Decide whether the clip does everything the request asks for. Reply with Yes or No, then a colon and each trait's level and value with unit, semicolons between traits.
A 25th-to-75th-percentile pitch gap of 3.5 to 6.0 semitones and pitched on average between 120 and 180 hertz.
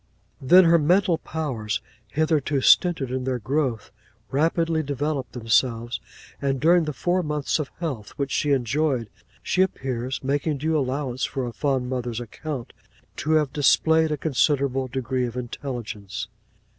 Yes: average, 3.8 semitones; low, 135 Hz